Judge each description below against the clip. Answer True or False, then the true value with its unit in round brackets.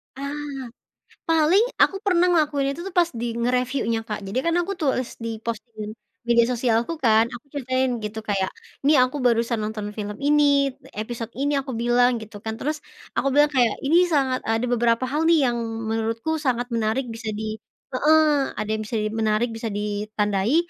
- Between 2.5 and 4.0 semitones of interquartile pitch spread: False (4.5 semitones)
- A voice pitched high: True (240 Hz)